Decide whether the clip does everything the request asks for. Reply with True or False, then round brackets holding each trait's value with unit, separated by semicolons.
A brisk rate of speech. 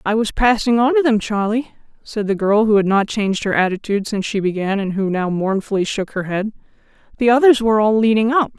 True (225 wpm)